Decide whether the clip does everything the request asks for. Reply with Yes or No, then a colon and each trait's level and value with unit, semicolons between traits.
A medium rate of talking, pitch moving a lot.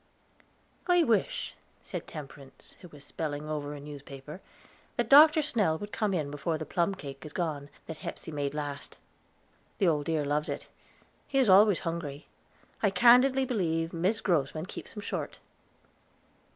Yes: average, 155 wpm; wide, 6.0 semitones